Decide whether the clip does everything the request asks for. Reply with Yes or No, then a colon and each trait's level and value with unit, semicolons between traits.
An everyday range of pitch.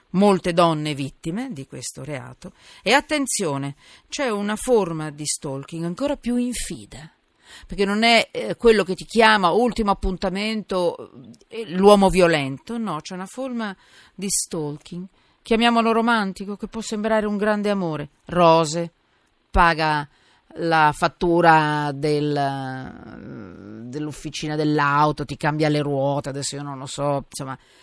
No: wide, 6.1 semitones